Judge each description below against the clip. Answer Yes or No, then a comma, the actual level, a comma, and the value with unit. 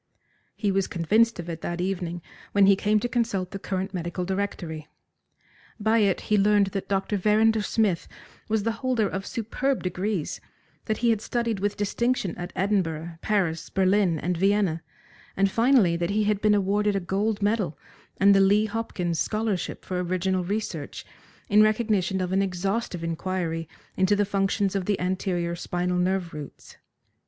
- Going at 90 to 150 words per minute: No, average, 165 wpm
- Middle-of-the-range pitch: No, high, 195 Hz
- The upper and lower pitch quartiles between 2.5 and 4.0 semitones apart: Yes, average, 2.8 semitones